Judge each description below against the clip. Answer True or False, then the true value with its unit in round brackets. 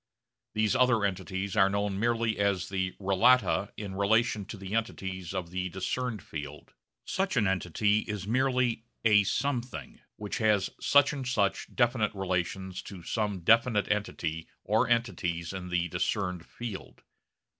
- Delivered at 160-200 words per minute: False (145 wpm)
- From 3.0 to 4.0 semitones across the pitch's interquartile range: True (3.5 semitones)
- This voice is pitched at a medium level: False (100 Hz)